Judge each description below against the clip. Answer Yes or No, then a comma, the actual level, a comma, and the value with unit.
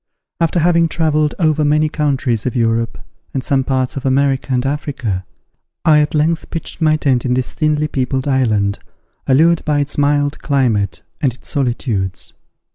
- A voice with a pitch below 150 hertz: Yes, medium, 140 Hz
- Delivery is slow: No, average, 160 wpm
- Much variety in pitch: No, average, 3.3 semitones